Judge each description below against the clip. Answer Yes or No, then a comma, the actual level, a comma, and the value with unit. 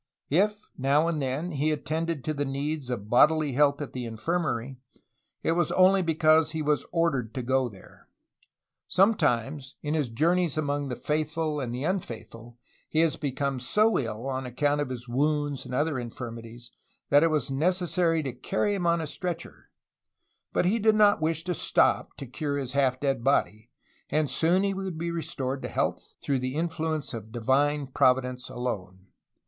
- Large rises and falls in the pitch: No, average, 4.3 semitones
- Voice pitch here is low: No, medium, 145 Hz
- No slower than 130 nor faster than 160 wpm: No, average, 175 wpm